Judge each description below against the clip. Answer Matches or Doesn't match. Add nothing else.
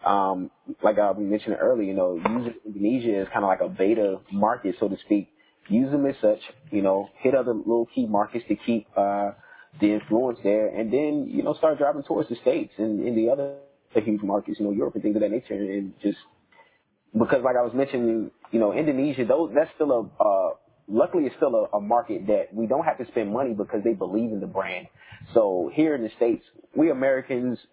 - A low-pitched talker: Matches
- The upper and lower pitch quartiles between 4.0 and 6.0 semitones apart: Matches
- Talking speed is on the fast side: Matches